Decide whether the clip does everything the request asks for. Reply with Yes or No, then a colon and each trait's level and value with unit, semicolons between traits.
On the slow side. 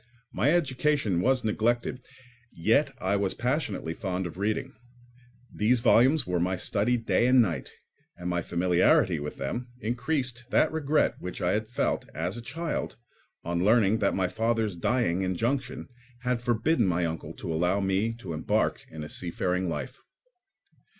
No: average, 155 wpm